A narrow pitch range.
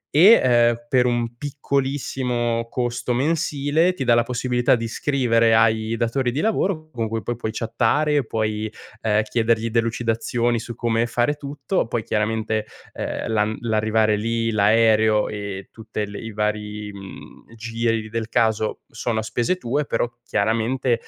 Yes: narrow, 2.2 semitones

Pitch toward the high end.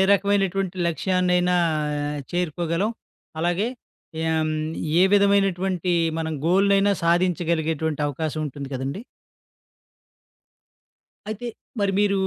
No: medium, 180 Hz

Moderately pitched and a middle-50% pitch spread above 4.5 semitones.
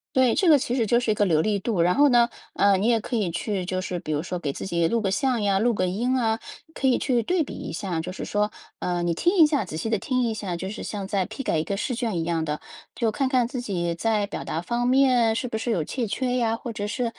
No: high, 215 Hz; average, 4.9 semitones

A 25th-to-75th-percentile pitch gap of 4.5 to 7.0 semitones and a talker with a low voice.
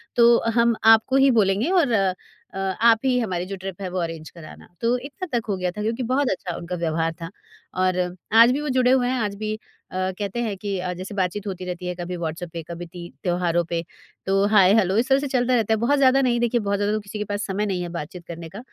No: average, 4.8 semitones; high, 200 Hz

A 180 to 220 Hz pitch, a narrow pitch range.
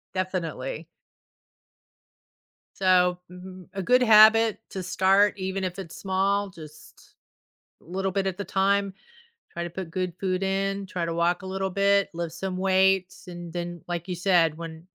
Yes: medium, 185 Hz; narrow, 1.9 semitones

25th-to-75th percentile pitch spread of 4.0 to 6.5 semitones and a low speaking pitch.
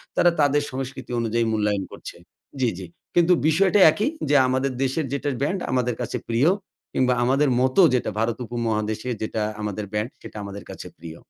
Yes: average, 4.6 semitones; low, 125 Hz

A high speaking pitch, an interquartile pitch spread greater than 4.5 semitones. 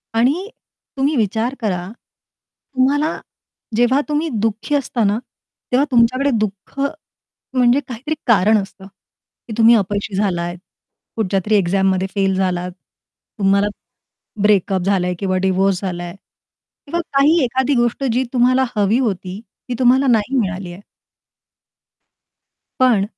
Yes: high, 220 Hz; average, 5.0 semitones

